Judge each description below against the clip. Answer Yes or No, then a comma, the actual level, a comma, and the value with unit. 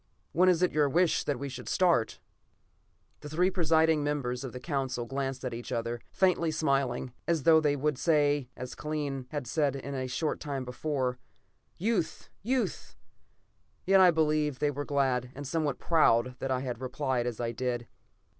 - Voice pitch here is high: No, medium, 140 Hz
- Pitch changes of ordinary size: Yes, average, 3.7 semitones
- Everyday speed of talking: Yes, average, 175 wpm